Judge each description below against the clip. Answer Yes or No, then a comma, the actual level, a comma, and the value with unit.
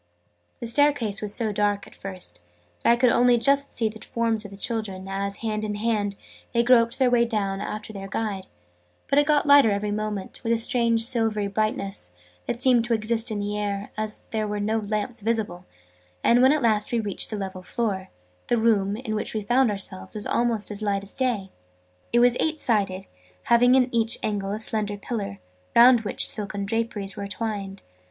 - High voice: Yes, high, 215 Hz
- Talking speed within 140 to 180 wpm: No, average, 200 wpm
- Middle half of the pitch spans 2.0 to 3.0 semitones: Yes, narrow, 2.6 semitones